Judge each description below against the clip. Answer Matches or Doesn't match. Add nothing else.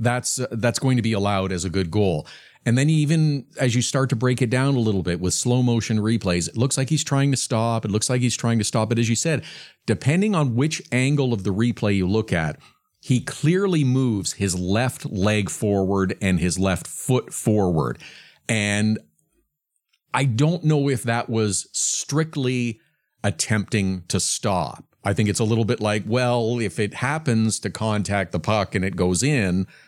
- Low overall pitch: Matches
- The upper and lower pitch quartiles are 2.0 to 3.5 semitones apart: Doesn't match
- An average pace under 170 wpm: Doesn't match